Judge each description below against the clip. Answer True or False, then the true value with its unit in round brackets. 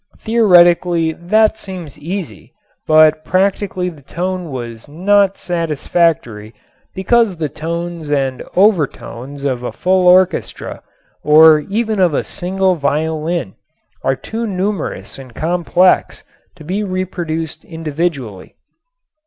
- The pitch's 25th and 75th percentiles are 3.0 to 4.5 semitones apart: True (3.7 semitones)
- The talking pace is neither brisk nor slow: False (110 wpm)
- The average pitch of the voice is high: False (170 Hz)